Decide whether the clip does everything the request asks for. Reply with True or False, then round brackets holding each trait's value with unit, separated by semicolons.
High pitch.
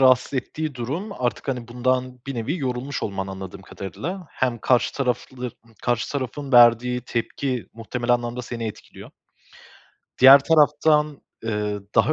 False (125 Hz)